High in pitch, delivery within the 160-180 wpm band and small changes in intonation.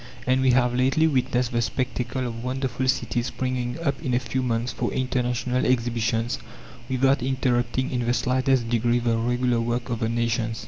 No: low, 125 Hz; average, 175 wpm; narrow, 1.5 semitones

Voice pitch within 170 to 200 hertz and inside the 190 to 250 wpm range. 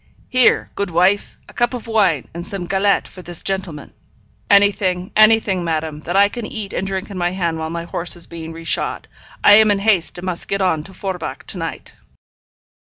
Yes: medium, 185 Hz; average, 200 wpm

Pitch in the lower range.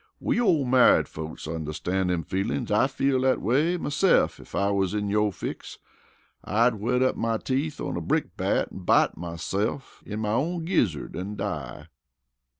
Yes: low, 110 Hz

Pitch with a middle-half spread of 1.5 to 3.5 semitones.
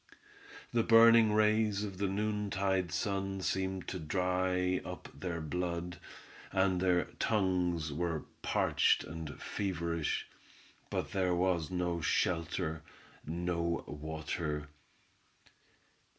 Yes: narrow, 2.5 semitones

